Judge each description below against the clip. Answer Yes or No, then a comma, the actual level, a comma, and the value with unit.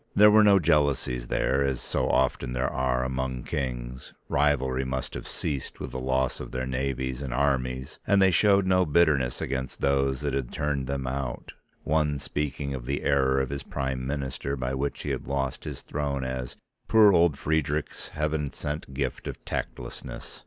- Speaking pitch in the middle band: No, very low, 70 Hz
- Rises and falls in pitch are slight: Yes, narrow, 2.2 semitones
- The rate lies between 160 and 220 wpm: Yes, average, 180 wpm